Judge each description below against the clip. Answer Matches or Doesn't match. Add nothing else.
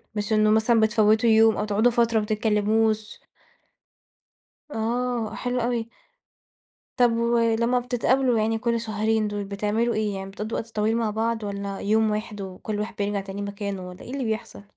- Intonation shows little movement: Matches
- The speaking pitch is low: Doesn't match